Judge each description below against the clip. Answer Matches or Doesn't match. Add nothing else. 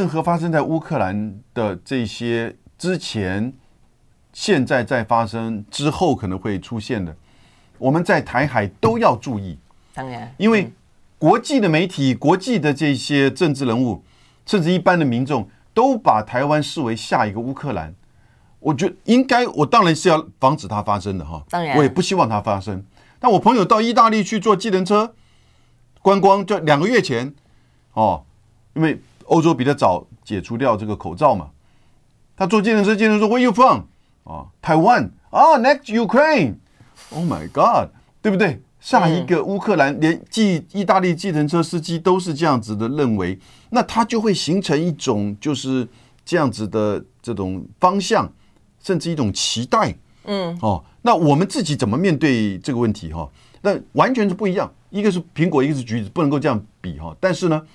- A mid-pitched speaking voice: Matches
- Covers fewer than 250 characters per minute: Doesn't match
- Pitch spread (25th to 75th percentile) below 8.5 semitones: Doesn't match